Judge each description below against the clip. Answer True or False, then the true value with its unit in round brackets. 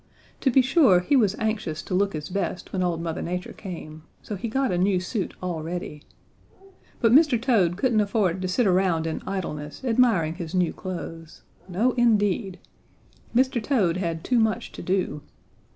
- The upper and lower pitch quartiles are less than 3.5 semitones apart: False (4.9 semitones)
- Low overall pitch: False (190 Hz)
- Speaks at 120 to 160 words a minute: False (175 wpm)